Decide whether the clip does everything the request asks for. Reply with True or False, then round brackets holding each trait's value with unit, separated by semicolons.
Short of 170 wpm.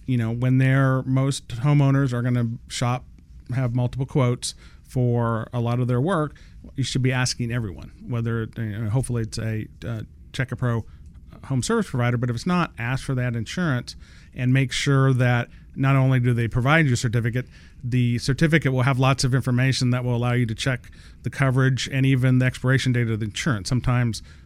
False (200 wpm)